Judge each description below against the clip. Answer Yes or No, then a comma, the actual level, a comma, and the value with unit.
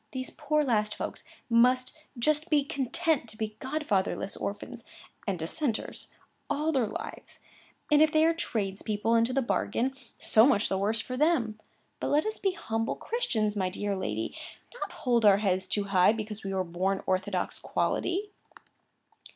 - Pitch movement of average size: No, wide, 6.3 semitones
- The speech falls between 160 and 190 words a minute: Yes, average, 165 wpm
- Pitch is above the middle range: Yes, high, 230 Hz